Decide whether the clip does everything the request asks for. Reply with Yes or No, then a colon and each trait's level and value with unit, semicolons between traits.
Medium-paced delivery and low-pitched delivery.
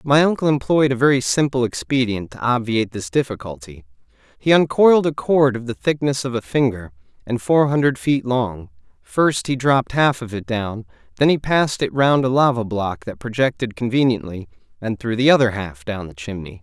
Yes: average, 190 wpm; low, 125 Hz